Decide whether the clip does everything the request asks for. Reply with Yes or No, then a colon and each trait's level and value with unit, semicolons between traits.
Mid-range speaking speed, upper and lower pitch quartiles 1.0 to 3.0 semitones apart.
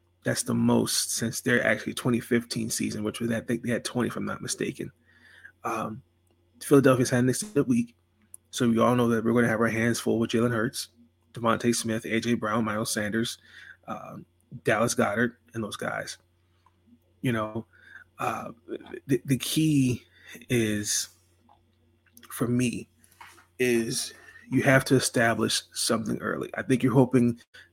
Yes: average, 155 wpm; narrow, 2.4 semitones